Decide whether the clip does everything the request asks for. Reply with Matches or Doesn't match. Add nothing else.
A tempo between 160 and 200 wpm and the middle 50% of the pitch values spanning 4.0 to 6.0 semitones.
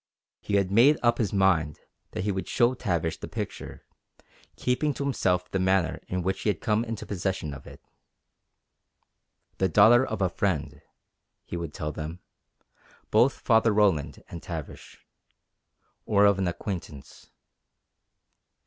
Doesn't match